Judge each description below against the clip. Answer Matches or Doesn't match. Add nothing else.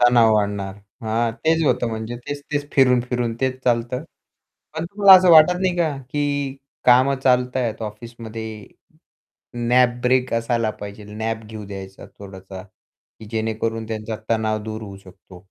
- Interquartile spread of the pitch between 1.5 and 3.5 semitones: Matches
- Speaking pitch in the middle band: Doesn't match